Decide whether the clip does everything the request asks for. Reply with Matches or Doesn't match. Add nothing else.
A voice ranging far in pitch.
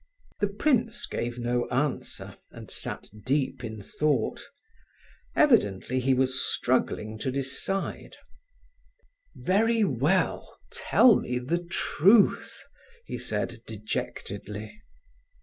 Matches